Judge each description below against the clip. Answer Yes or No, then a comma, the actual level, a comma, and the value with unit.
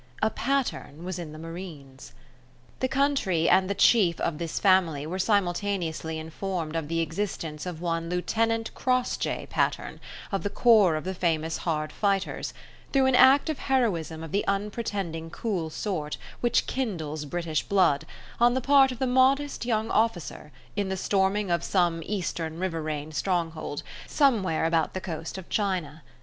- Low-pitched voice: No, medium, 185 Hz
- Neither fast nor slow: Yes, average, 160 wpm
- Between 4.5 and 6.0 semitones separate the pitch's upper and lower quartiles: Yes, average, 5.0 semitones